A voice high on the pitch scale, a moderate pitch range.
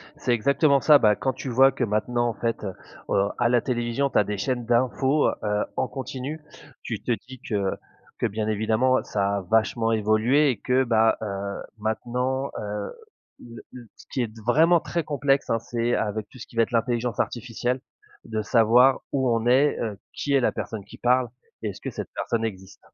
No: low, 120 Hz; average, 3.2 semitones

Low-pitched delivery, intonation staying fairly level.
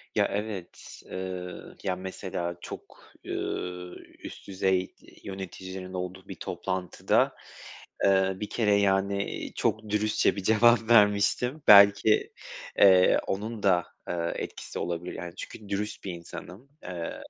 Yes: very low, 95 Hz; narrow, 2.1 semitones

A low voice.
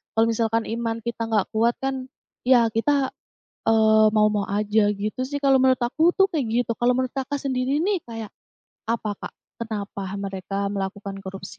No: high, 225 Hz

